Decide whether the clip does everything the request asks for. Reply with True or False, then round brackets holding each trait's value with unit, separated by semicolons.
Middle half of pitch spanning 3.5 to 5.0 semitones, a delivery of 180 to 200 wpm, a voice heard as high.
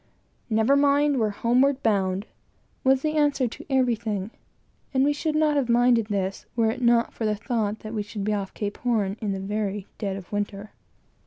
True (4.2 semitones; 190 wpm; 225 Hz)